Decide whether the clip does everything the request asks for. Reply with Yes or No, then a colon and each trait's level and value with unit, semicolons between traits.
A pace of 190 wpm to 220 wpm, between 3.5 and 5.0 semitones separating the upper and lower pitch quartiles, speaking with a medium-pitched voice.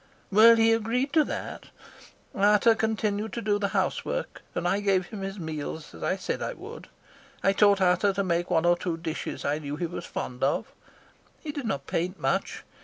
No: average, 195 wpm; average, 4.3 semitones; high, 195 Hz